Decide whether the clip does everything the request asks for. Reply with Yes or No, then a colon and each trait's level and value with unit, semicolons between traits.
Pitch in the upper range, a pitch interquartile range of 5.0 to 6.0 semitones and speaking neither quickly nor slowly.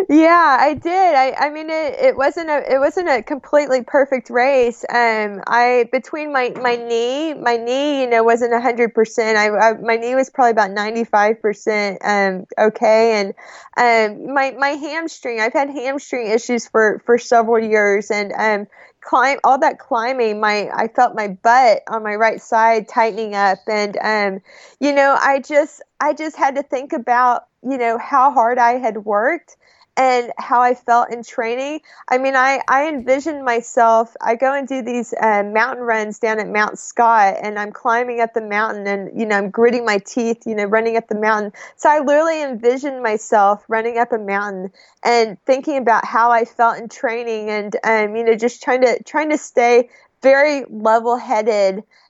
No: high, 235 Hz; average, 3.4 semitones; average, 185 wpm